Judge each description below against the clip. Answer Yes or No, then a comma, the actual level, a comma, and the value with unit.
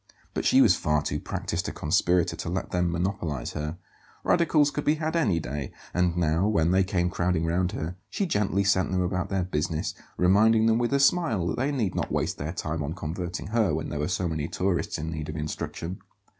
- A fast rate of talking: Yes, fast, 215 wpm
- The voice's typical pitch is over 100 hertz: No, very low, 90 Hz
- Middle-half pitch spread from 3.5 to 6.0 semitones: Yes, average, 3.9 semitones